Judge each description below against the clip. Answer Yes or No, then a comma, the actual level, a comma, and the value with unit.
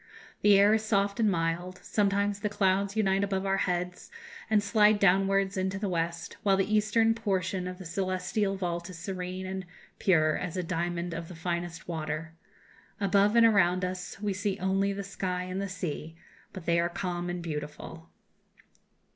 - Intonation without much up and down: Yes, narrow, 2.3 semitones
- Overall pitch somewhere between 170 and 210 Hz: Yes, high, 190 Hz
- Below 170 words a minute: No, average, 175 wpm